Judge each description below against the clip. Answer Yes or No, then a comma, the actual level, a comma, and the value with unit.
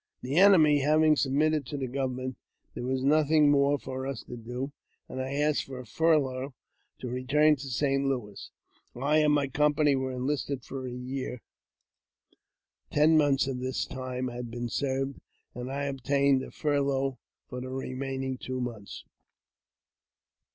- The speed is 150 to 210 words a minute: Yes, average, 165 wpm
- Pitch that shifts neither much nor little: No, narrow, 2.0 semitones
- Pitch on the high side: No, low, 135 Hz